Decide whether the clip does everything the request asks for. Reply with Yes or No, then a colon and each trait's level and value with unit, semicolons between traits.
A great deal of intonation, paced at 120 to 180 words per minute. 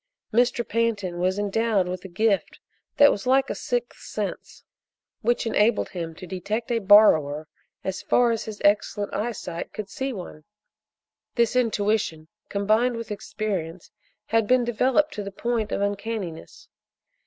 No: average, 3.4 semitones; average, 145 wpm